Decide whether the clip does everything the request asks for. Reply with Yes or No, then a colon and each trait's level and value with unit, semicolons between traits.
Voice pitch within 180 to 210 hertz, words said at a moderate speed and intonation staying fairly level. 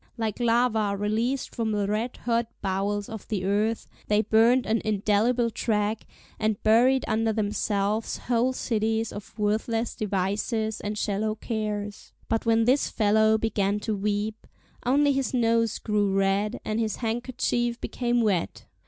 No: high, 220 Hz; average, 145 wpm; narrow, 2.0 semitones